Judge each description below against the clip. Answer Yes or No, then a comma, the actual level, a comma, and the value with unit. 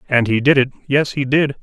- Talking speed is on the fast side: Yes, fast, 260 wpm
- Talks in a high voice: No, low, 135 Hz